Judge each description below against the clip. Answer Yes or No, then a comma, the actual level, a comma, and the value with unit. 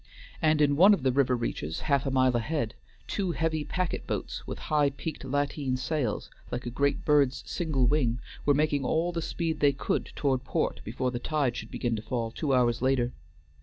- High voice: No, medium, 140 Hz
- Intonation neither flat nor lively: Yes, average, 3.5 semitones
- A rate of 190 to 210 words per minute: Yes, average, 200 wpm